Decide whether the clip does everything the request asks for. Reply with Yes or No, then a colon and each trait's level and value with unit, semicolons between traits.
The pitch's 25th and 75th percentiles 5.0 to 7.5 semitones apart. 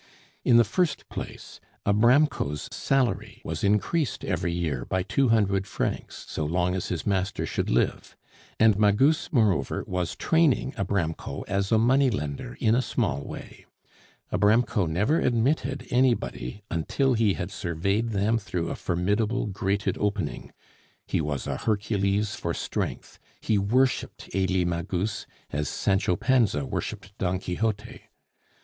No: average, 4.6 semitones